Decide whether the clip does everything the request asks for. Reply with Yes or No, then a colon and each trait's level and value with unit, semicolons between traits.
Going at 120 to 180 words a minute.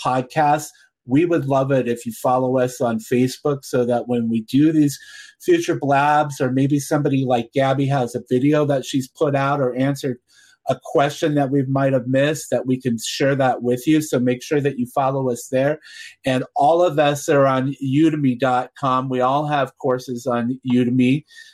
No: average, 190 wpm